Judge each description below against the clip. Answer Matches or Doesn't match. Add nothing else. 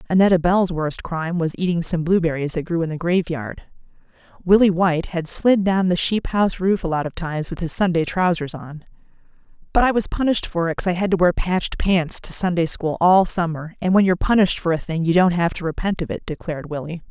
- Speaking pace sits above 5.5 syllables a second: Matches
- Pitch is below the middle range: Doesn't match